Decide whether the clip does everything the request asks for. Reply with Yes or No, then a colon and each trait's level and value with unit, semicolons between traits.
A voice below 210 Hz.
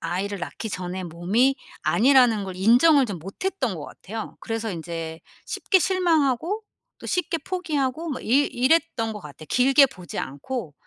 No: high, 235 Hz